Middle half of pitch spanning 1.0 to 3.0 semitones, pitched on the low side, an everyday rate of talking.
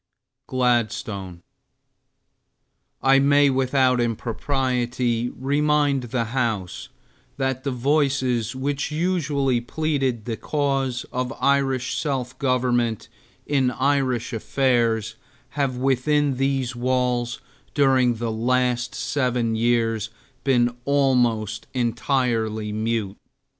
No: narrow, 2.5 semitones; low, 125 Hz; slow, 90 wpm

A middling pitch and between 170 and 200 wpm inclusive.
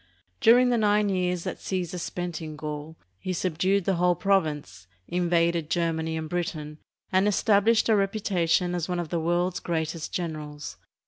No: medium, 175 Hz; average, 160 wpm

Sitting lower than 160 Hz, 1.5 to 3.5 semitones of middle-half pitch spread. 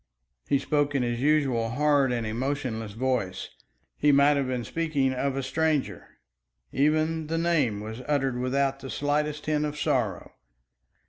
Yes: medium, 140 Hz; average, 3.2 semitones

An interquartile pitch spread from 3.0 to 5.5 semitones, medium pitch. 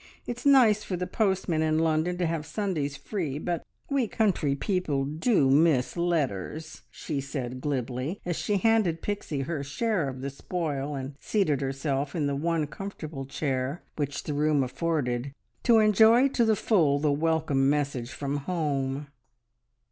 Yes: average, 4.7 semitones; medium, 155 Hz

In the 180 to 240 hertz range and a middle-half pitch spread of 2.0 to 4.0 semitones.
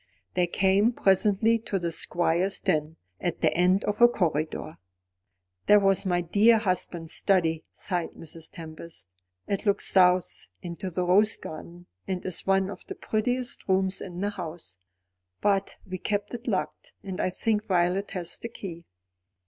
Yes: medium, 185 Hz; average, 2.8 semitones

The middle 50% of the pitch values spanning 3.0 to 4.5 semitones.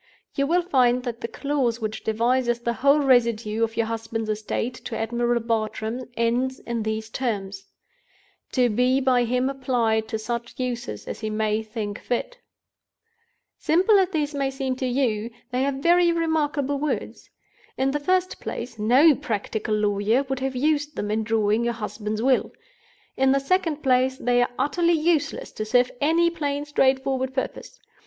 Yes: average, 3.8 semitones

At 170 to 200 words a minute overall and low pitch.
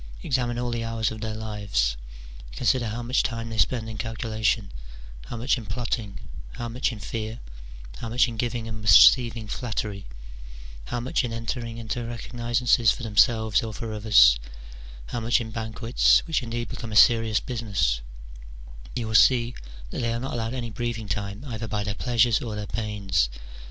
Yes: average, 175 wpm; low, 115 Hz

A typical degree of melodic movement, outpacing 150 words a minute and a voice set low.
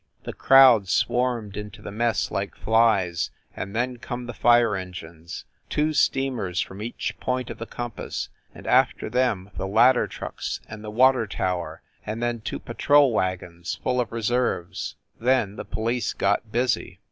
Yes: average, 3.9 semitones; average, 165 wpm; low, 115 Hz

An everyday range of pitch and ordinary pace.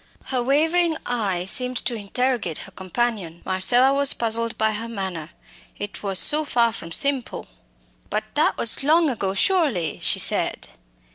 No: wide, 5.7 semitones; average, 150 wpm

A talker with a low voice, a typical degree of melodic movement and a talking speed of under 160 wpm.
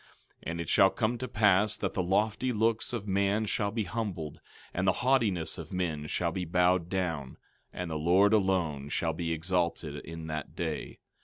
No: very low, 90 Hz; average, 4.0 semitones; average, 185 wpm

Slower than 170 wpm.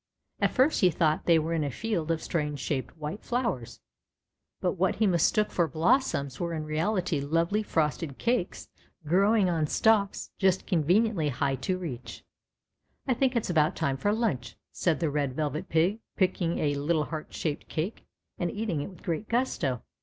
No: average, 175 wpm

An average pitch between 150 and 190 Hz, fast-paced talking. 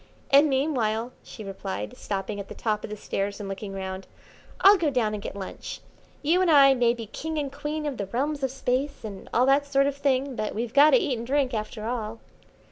No: very high, 250 Hz; fast, 225 wpm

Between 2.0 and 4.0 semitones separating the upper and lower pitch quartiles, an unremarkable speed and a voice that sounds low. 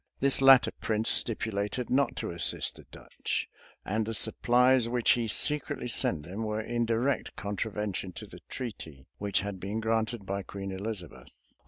Yes: average, 3.2 semitones; average, 160 wpm; low, 110 Hz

